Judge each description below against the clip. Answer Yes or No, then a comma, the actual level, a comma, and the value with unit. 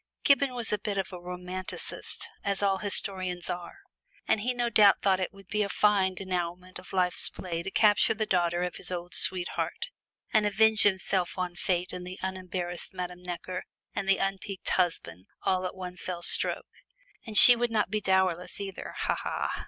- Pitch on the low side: No, medium, 185 Hz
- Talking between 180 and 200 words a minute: Yes, average, 185 wpm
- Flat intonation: Yes, narrow, 2.1 semitones